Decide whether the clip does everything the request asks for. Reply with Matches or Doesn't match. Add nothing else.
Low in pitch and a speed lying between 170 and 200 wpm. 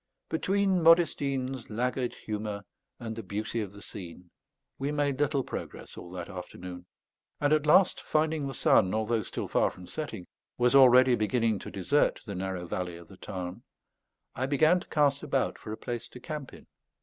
Matches